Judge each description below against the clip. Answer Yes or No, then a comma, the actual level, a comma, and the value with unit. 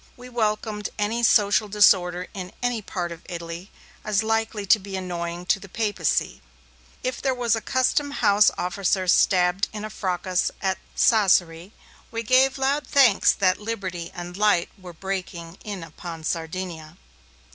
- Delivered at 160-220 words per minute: No, average, 150 wpm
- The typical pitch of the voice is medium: No, high, 195 Hz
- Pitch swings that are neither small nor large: Yes, average, 3.6 semitones